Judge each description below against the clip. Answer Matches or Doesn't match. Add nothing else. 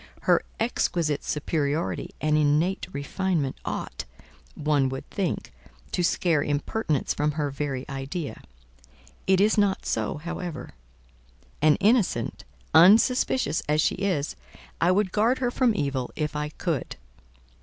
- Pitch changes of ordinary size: Matches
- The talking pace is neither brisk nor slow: Doesn't match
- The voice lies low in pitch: Doesn't match